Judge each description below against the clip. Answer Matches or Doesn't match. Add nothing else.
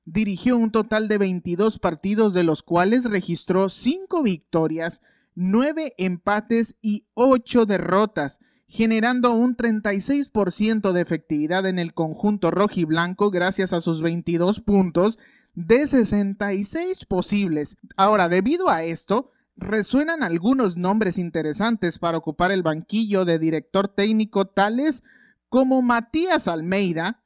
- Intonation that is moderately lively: Matches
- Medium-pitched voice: Doesn't match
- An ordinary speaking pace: Doesn't match